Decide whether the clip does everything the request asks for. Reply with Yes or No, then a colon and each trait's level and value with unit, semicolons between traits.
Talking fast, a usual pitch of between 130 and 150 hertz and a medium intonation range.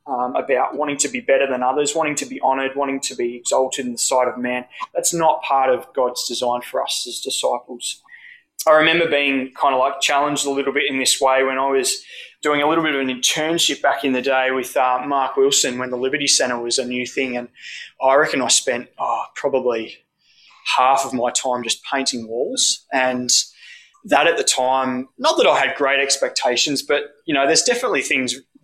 Yes: fast, 210 wpm; low, 135 Hz; average, 3.3 semitones